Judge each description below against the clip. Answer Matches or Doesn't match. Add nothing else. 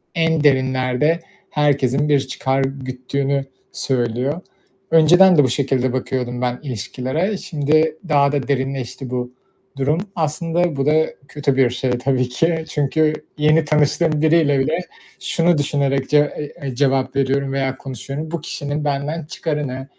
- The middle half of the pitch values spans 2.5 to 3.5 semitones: Matches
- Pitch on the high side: Doesn't match